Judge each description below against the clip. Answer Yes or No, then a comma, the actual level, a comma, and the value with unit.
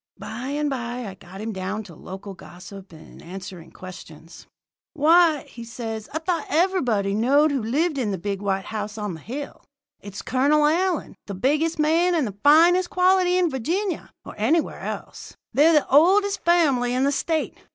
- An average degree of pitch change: No, wide, 8.1 semitones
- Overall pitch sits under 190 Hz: No, very high, 260 Hz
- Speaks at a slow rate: No, average, 175 wpm